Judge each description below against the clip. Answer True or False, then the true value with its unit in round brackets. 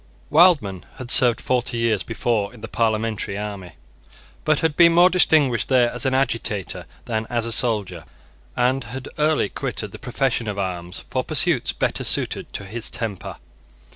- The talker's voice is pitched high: False (120 Hz)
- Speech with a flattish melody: False (4.1 semitones)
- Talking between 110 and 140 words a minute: False (165 wpm)